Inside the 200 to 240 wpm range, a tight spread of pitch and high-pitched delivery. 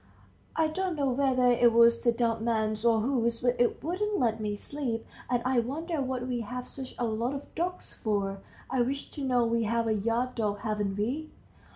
No: fast, 205 wpm; average, 3.0 semitones; high, 240 Hz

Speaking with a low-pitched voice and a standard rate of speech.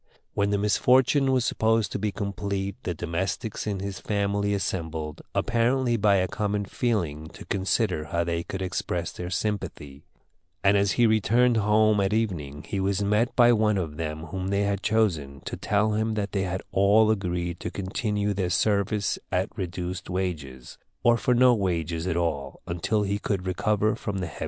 Yes: low, 100 Hz; average, 180 wpm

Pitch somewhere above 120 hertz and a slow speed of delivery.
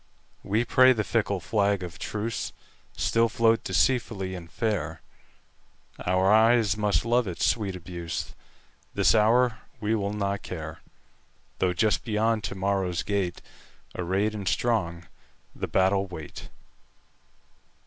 No: low, 100 Hz; slow, 105 wpm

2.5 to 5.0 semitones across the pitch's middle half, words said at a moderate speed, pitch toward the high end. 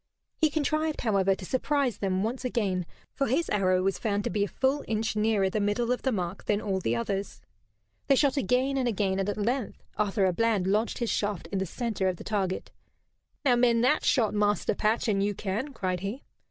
No: average, 4.3 semitones; fast, 215 wpm; high, 210 Hz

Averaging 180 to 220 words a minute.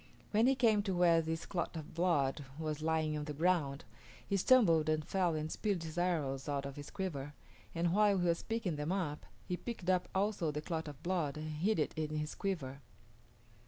Yes: fast, 205 wpm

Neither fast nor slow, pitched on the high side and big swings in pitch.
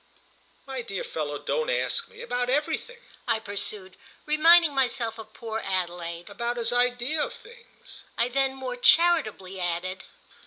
Yes: average, 145 wpm; high, 245 Hz; wide, 7.5 semitones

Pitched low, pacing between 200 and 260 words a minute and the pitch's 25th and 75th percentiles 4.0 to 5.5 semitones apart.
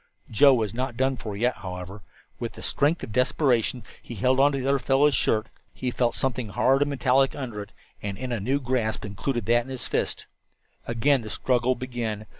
No: low, 125 Hz; fast, 205 wpm; average, 3.3 semitones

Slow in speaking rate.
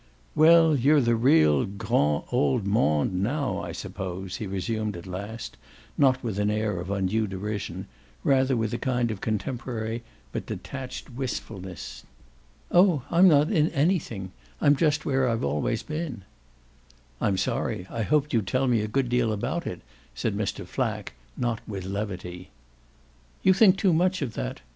No: average, 160 wpm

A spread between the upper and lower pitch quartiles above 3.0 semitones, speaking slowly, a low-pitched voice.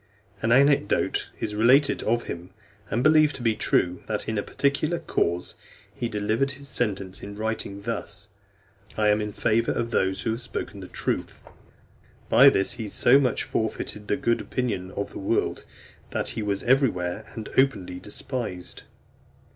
No: average, 3.9 semitones; average, 165 wpm; low, 110 Hz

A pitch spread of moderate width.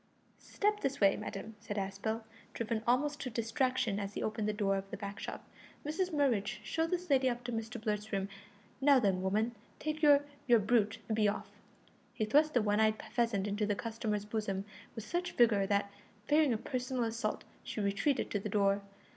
Yes: average, 3.9 semitones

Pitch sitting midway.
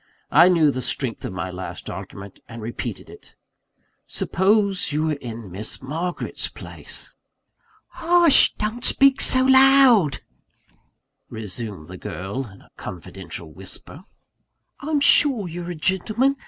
Yes: medium, 150 Hz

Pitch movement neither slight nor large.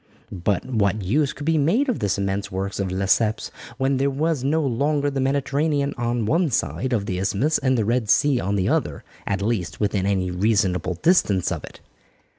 No: wide, 6.2 semitones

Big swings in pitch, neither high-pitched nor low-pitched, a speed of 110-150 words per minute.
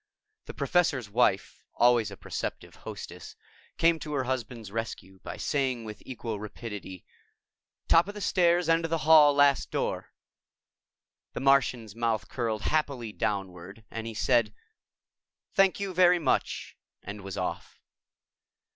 No: wide, 6.5 semitones; low, 120 Hz; average, 140 wpm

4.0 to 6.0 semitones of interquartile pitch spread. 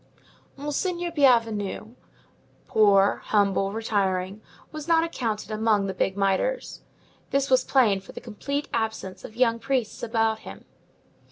Yes: average, 5.1 semitones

